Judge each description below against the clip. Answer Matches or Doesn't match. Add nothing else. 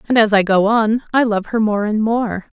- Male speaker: Doesn't match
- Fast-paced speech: Matches